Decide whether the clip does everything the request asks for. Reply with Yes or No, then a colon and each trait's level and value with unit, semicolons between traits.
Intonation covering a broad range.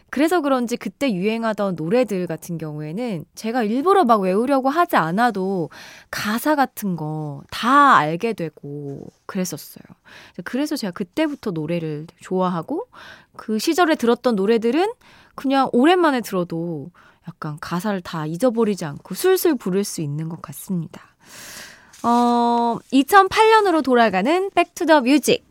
Yes: wide, 8.2 semitones